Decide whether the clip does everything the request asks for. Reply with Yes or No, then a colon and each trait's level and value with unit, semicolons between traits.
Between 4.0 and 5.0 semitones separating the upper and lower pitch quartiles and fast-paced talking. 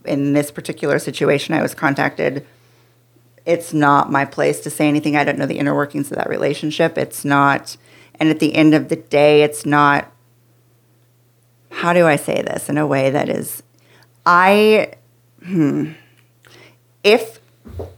No: average, 4.3 semitones; average, 155 wpm